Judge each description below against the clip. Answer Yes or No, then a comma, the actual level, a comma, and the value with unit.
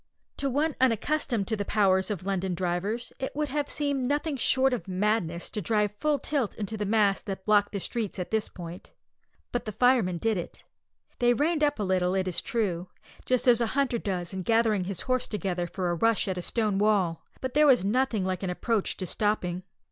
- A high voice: Yes, high, 210 Hz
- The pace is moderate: No, fast, 210 wpm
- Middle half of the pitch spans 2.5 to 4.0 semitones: No, average, 4.9 semitones